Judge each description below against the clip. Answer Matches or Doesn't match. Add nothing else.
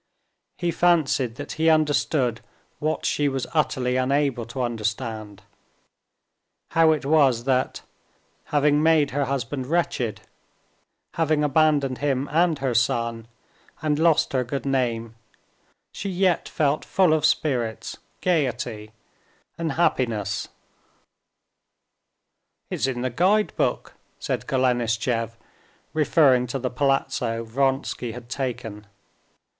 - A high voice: Doesn't match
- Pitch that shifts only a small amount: Doesn't match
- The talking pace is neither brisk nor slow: Doesn't match